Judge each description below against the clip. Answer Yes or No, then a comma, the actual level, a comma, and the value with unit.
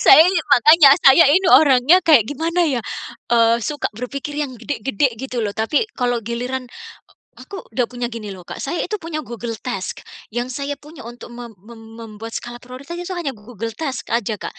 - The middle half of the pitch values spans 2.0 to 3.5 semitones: No, average, 4.4 semitones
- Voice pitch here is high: Yes, very high, 250 Hz